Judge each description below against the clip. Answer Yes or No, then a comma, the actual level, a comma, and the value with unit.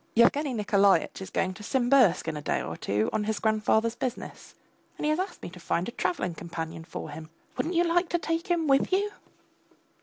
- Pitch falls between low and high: No, high, 220 Hz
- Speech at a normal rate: No, fast, 210 wpm